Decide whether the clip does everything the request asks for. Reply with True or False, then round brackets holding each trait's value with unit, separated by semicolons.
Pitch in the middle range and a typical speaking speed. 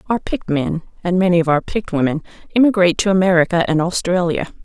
True (180 Hz; 180 wpm)